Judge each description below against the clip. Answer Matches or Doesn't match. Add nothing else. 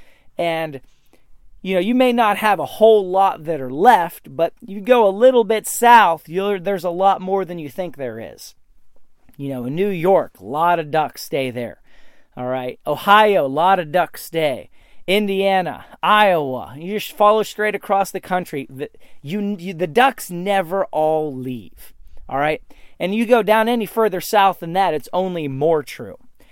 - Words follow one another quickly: Doesn't match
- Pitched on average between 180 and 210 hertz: Matches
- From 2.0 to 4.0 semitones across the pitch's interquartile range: Doesn't match